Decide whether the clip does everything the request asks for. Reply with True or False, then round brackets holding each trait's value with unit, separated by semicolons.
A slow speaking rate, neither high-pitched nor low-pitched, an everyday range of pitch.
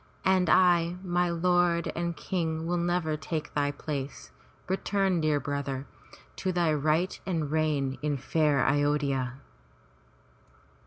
True (125 wpm; 160 Hz; 3.3 semitones)